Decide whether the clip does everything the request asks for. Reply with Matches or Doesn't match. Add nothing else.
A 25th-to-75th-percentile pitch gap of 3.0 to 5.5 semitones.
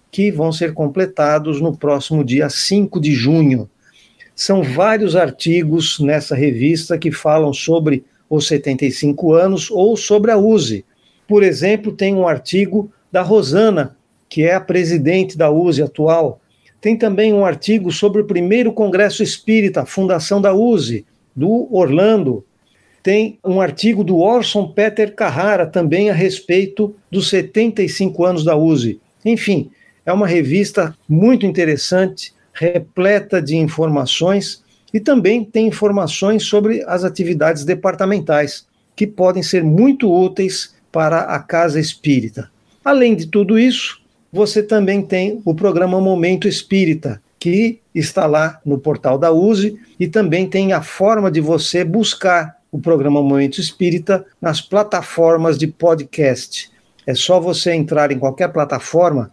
Matches